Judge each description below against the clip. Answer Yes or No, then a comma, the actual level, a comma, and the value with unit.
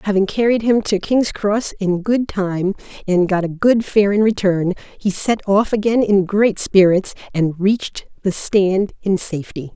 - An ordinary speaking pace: Yes, average, 180 wpm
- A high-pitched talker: Yes, high, 200 Hz